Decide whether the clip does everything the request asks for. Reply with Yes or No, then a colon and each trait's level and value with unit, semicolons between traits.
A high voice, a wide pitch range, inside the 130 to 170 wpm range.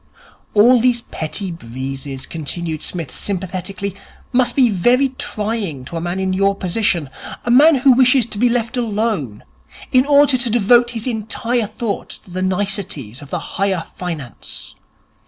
Yes: high, 205 Hz; wide, 5.9 semitones; average, 155 wpm